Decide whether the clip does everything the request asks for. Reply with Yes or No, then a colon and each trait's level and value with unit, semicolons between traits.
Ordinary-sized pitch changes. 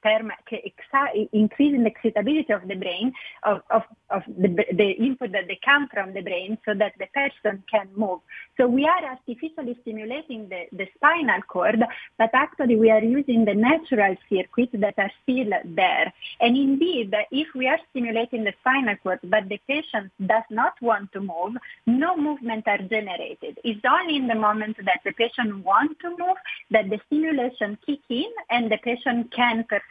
Yes: average, 4.2 semitones